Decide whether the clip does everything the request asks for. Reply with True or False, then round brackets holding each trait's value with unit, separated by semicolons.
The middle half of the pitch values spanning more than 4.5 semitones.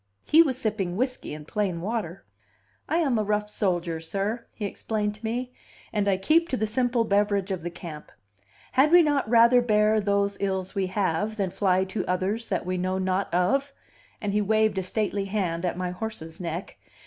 False (3.2 semitones)